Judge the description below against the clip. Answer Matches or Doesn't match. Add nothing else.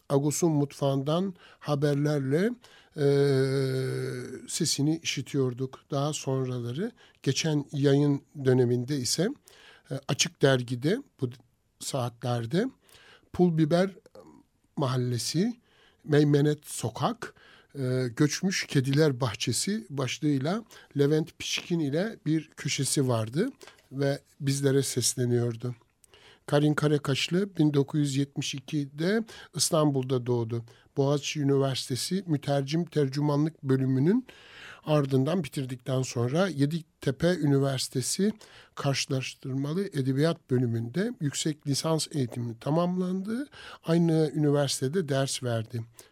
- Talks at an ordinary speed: Doesn't match